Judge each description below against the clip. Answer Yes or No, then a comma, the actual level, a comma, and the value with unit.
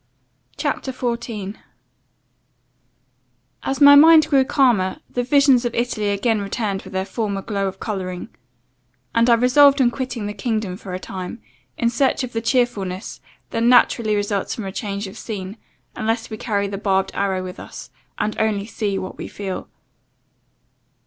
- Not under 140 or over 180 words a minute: Yes, average, 160 wpm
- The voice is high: Yes, high, 215 Hz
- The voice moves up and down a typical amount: Yes, average, 3.7 semitones